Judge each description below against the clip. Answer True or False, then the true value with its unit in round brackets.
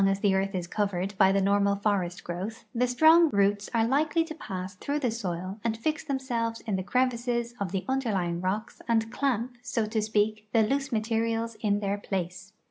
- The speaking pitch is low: False (215 Hz)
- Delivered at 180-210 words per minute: True (195 wpm)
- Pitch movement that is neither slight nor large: True (3.5 semitones)